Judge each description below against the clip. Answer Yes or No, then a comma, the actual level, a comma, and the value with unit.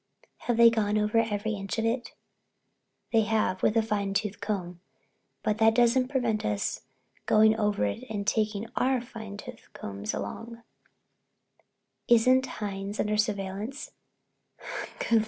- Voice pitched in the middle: No, high, 215 Hz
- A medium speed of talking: No, slow, 130 wpm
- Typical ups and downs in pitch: No, narrow, 2.2 semitones